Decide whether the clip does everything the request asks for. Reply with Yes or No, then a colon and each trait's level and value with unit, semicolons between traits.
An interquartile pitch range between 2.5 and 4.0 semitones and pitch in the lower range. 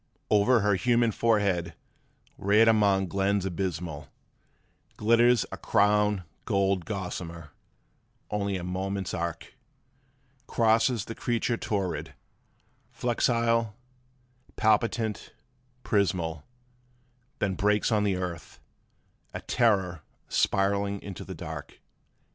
Yes: average, 3.2 semitones; low, 100 Hz